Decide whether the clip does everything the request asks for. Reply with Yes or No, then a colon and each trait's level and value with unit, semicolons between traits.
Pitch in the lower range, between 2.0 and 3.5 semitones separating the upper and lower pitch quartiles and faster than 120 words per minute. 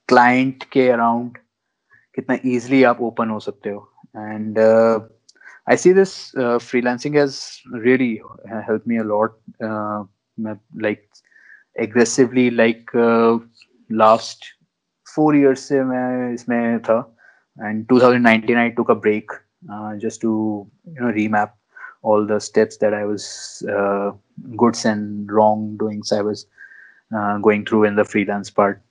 Yes: low, 110 Hz; narrow, 2.4 semitones; average, 140 wpm